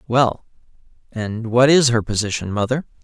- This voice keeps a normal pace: No, slow, 120 wpm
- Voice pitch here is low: Yes, low, 120 Hz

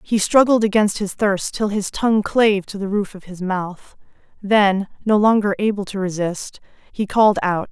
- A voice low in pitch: No, high, 200 Hz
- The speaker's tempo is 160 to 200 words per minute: Yes, average, 185 wpm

